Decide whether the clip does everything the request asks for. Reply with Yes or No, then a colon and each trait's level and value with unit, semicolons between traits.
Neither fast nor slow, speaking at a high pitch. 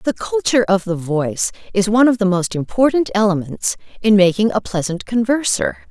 Yes: average, 175 wpm; high, 195 Hz